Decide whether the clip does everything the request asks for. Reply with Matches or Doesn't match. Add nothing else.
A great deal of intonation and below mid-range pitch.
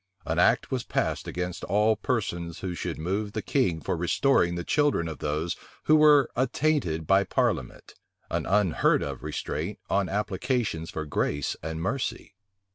Matches